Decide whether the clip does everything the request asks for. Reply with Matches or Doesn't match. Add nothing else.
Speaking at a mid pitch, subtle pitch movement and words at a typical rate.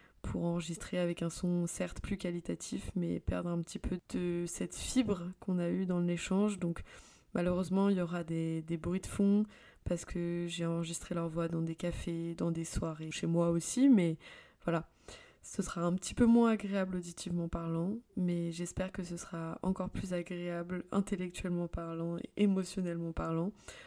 Matches